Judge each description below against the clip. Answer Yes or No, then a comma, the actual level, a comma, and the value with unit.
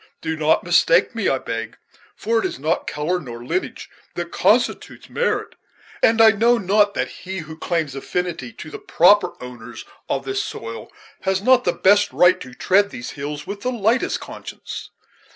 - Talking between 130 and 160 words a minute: No, average, 175 wpm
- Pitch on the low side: No, medium, 185 Hz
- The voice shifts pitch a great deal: Yes, wide, 6.7 semitones